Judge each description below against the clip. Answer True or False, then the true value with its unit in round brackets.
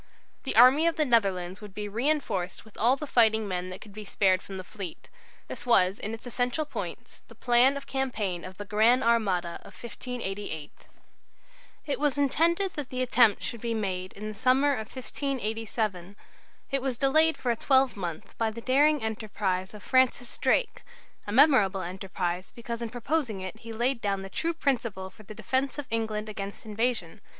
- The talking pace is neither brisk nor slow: True (180 wpm)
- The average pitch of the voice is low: False (225 Hz)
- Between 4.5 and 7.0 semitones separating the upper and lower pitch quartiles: True (4.8 semitones)